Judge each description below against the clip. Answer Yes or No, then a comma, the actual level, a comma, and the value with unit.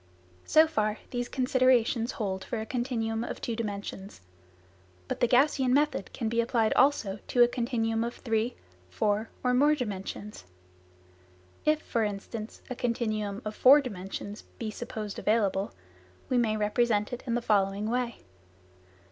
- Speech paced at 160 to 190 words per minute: No, average, 150 wpm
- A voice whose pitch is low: No, high, 230 Hz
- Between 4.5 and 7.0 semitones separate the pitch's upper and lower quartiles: No, average, 2.9 semitones